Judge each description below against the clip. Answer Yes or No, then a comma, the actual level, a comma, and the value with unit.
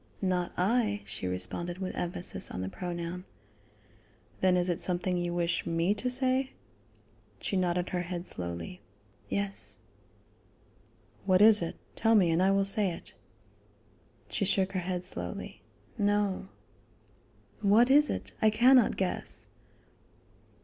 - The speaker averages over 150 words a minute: No, slow, 135 wpm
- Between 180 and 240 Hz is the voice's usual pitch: Yes, medium, 185 Hz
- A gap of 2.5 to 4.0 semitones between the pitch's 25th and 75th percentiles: Yes, average, 2.9 semitones